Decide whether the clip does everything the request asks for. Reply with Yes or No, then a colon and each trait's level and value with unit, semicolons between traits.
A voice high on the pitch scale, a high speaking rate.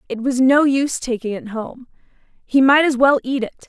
Yes: very high, 255 Hz; fast, 210 wpm